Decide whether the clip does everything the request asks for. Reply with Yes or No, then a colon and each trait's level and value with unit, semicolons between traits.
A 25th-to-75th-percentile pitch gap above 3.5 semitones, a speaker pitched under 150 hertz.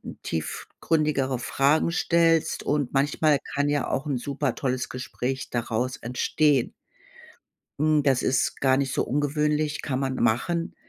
No: average, 2.8 semitones; medium, 140 Hz